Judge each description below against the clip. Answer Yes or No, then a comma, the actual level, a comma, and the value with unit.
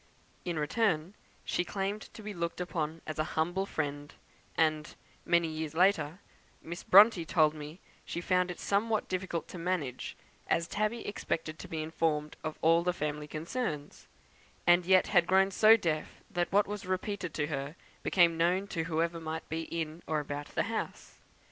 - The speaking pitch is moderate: Yes, medium, 170 Hz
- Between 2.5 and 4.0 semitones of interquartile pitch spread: Yes, average, 3.1 semitones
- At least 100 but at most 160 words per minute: No, average, 175 wpm